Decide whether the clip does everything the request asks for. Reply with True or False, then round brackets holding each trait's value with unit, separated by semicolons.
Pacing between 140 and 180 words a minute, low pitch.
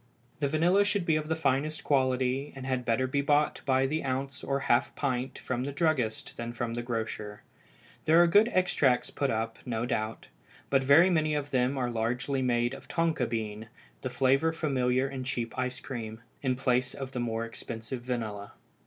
False (190 wpm; 130 Hz)